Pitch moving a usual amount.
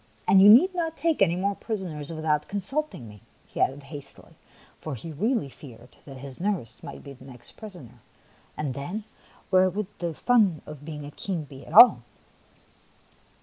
No: wide, 6.6 semitones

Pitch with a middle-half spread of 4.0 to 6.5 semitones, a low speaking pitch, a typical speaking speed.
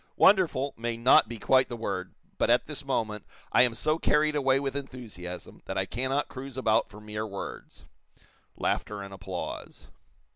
Yes: average, 4.3 semitones; low, 120 Hz; average, 170 wpm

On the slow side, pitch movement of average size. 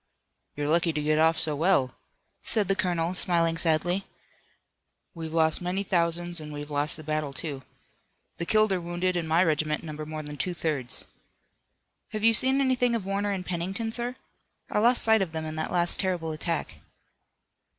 No: average, 180 wpm; average, 3.6 semitones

